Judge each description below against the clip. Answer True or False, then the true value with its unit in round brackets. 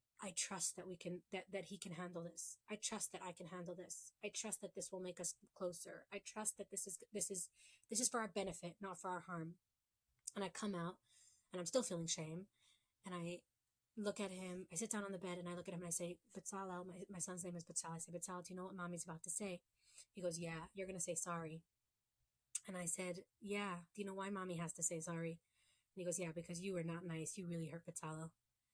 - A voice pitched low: False (180 Hz)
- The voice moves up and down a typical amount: False (2.2 semitones)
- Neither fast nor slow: False (255 wpm)